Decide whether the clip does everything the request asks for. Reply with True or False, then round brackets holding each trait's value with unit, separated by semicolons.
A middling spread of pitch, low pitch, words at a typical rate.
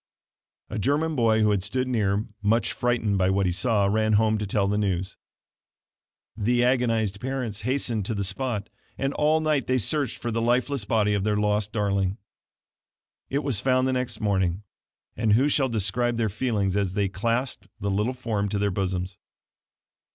True (3.7 semitones; 110 Hz; 180 wpm)